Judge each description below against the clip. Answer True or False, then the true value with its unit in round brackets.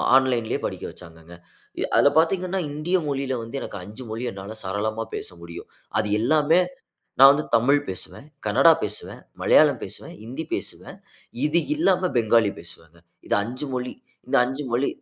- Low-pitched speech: True (125 Hz)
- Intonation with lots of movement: True (5.7 semitones)